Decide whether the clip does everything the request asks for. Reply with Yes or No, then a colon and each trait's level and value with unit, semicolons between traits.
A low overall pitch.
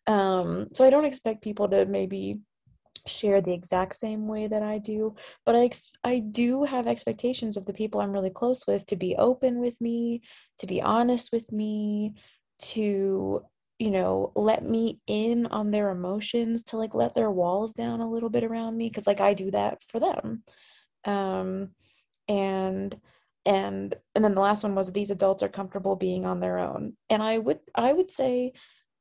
No: high, 210 Hz